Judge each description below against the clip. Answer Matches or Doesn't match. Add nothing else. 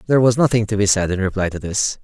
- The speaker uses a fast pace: Matches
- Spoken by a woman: Doesn't match